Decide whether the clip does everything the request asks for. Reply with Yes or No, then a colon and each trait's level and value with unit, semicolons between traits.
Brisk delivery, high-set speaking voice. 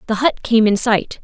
Yes: fast, 245 wpm; high, 225 Hz